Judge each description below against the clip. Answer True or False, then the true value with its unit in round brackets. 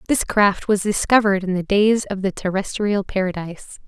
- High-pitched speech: True (200 Hz)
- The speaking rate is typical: True (170 wpm)